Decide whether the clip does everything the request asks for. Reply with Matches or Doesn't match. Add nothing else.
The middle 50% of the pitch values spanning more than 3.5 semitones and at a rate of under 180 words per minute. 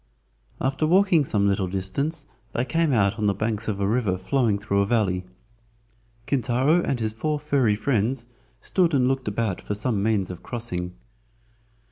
Matches